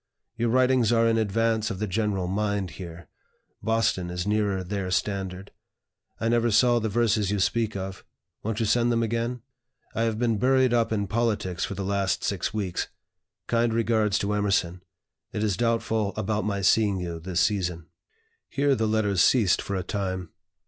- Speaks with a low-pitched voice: Yes, low, 105 Hz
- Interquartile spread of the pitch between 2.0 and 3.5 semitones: Yes, average, 3.0 semitones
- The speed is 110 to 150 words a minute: No, average, 175 wpm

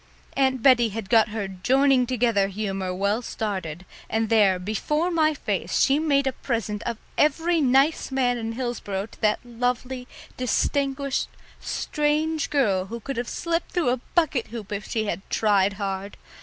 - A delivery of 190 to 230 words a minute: No, average, 160 wpm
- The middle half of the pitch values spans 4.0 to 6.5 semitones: Yes, average, 4.9 semitones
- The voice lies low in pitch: No, high, 240 Hz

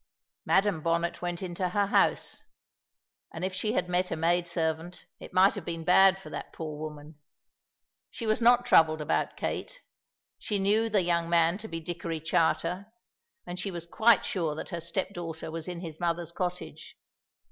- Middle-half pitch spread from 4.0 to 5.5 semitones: No, average, 2.7 semitones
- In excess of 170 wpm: Yes, average, 180 wpm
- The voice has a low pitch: No, medium, 175 Hz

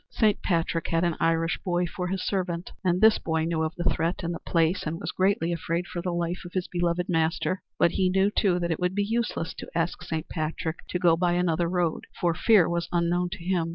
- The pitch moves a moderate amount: No, narrow, 1.6 semitones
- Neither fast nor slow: No, fast, 235 wpm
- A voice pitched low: No, medium, 175 Hz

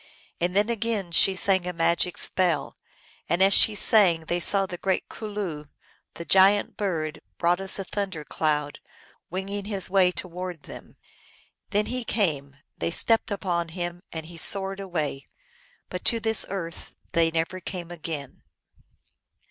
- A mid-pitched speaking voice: Yes, medium, 180 Hz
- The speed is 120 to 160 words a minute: Yes, average, 155 wpm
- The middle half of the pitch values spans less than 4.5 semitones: Yes, average, 3.0 semitones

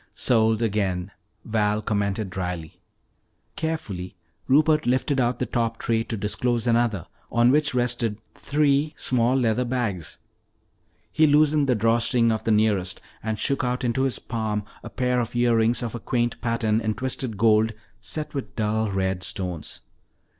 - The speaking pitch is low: Yes, low, 115 Hz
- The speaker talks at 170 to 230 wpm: No, average, 155 wpm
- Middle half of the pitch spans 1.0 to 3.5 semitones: Yes, average, 2.9 semitones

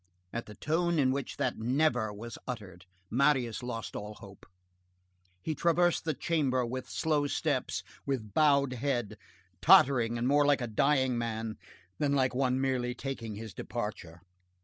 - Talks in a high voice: No, low, 130 Hz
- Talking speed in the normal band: Yes, average, 150 wpm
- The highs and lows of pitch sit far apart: No, average, 3.8 semitones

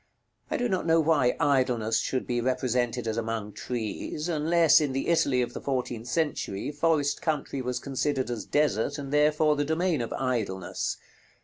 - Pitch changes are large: No, average, 4.0 semitones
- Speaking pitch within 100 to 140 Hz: Yes, low, 135 Hz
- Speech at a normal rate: Yes, average, 170 wpm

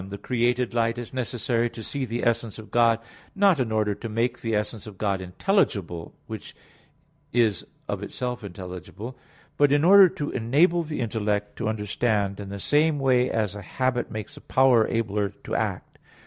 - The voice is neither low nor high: No, low, 115 Hz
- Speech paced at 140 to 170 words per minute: No, average, 180 wpm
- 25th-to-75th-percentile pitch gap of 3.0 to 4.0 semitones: Yes, average, 3.6 semitones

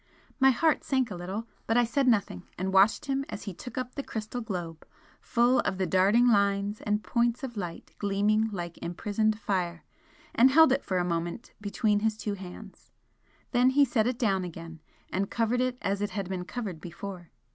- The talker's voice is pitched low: No, high, 210 Hz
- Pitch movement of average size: Yes, average, 4.3 semitones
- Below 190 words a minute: No, average, 195 wpm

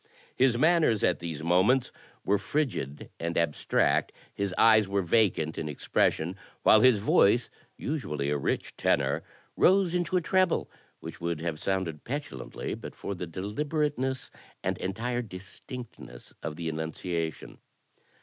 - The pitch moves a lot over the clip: Yes, wide, 7.6 semitones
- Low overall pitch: Yes, low, 100 Hz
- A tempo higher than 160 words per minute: No, slow, 135 wpm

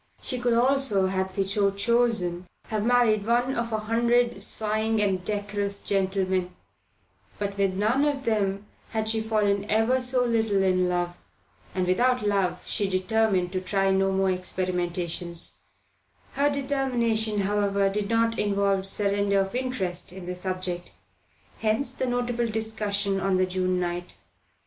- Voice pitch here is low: No, high, 205 Hz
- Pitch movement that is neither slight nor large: Yes, average, 3.3 semitones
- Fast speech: No, average, 145 wpm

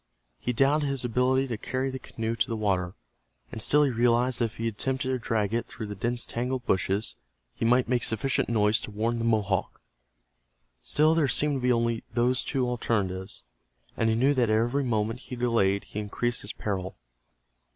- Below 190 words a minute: No, average, 195 wpm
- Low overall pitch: Yes, low, 115 Hz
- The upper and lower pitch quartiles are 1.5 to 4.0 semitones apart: Yes, average, 2.9 semitones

